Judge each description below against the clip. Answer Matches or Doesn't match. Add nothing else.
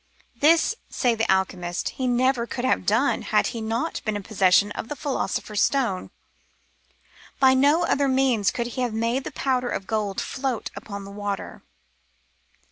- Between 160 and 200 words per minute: Matches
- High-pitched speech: Matches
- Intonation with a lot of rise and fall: Doesn't match